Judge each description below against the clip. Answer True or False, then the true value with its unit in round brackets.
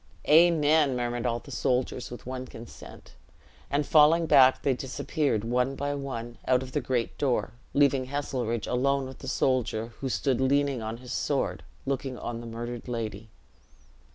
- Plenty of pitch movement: False (2.8 semitones)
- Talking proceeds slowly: False (160 wpm)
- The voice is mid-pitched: False (130 Hz)